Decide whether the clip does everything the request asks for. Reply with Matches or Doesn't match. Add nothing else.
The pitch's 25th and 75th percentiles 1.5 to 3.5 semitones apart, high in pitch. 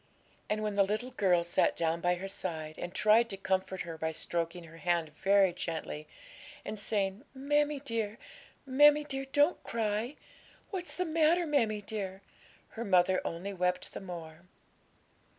Doesn't match